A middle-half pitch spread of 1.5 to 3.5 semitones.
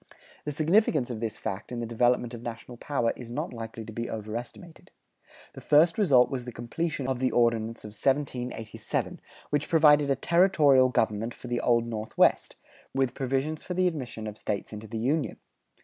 No: average, 4.2 semitones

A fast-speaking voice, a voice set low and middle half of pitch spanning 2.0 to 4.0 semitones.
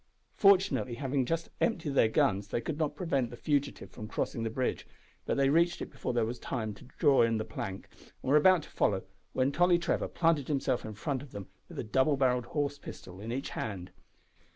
No: fast, 215 wpm; low, 130 Hz; average, 4.8 semitones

